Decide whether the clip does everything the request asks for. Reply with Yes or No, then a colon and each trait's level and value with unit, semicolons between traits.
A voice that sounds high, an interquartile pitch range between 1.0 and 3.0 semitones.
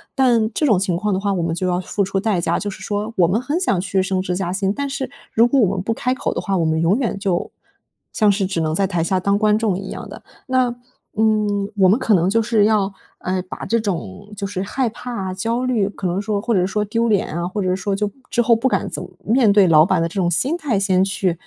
No: high, 200 Hz; average, 3.4 semitones